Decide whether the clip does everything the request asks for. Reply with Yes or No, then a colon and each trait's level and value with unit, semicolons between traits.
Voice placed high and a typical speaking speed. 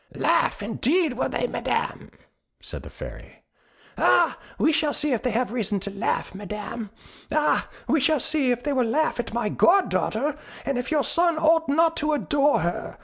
Yes: very high, 280 Hz; average, 180 wpm